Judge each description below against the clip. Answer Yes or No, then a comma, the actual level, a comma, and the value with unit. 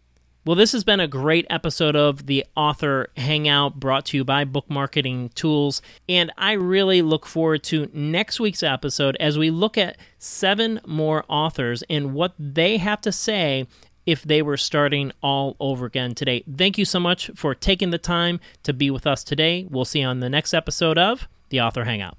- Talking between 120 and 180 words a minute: No, average, 195 wpm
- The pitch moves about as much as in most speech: Yes, average, 4.0 semitones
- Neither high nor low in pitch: Yes, medium, 150 Hz